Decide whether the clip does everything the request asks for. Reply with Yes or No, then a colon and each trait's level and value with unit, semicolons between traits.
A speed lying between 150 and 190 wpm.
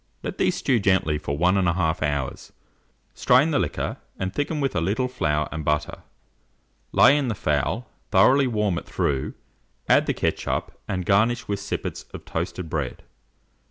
Yes: average, 160 wpm